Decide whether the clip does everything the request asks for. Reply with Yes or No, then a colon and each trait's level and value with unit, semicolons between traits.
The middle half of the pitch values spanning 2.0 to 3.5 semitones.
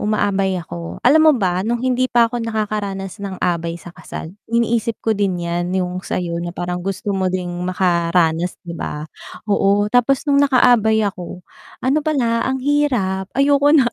No: average, 5.0 semitones